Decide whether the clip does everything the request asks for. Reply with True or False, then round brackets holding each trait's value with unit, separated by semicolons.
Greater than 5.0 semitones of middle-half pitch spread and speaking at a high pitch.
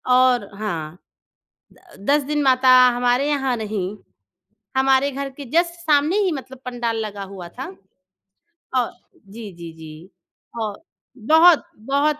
True (5.5 semitones; 255 Hz)